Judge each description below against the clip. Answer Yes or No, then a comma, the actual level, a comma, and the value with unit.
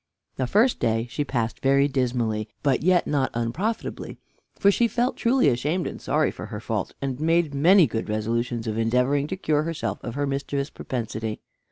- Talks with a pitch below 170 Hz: Yes, medium, 140 Hz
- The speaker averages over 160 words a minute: Yes, average, 180 wpm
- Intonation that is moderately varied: No, wide, 5.7 semitones